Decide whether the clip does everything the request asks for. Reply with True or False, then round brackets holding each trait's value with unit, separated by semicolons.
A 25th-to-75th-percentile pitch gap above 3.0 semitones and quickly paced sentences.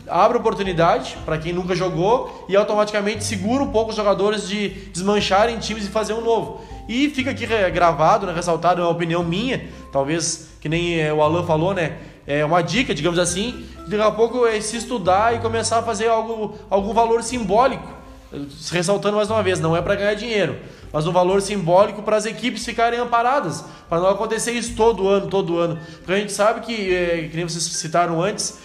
True (4.5 semitones; 195 wpm)